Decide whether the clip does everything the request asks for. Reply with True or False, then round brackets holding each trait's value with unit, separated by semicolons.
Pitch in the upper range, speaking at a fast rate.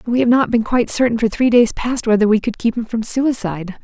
True (230 Hz; 265 wpm)